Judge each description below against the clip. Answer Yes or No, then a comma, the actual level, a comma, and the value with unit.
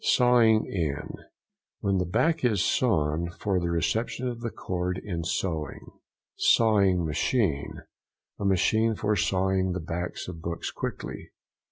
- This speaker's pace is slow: Yes, slow, 125 wpm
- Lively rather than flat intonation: No, average, 4.4 semitones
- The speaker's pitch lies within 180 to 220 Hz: No, very low, 95 Hz